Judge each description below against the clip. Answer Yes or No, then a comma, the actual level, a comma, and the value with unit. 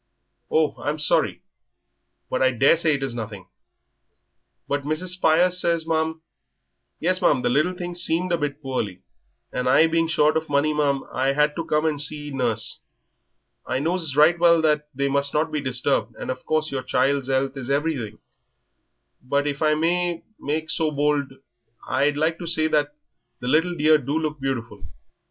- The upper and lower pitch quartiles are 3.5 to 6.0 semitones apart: No, average, 2.9 semitones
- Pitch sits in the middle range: Yes, medium, 150 Hz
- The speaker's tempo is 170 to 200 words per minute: Yes, average, 175 wpm